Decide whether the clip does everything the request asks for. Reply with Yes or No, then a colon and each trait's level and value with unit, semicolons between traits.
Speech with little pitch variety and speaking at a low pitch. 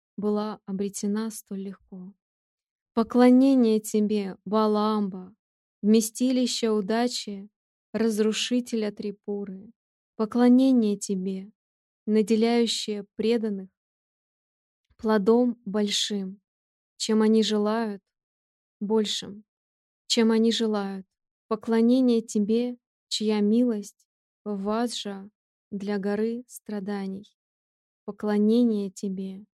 No: narrow, 1.8 semitones; high, 215 Hz